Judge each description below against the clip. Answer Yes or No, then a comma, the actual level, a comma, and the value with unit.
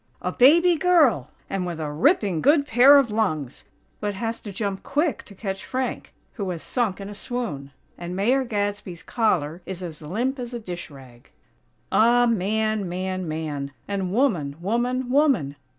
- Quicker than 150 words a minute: Yes, average, 170 wpm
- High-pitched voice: Yes, high, 205 Hz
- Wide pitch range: Yes, wide, 5.9 semitones